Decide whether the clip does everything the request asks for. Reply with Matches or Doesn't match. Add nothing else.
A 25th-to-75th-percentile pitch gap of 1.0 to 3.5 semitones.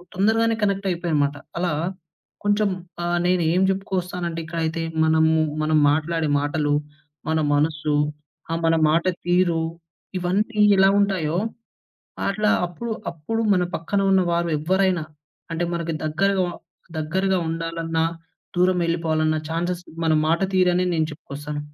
Matches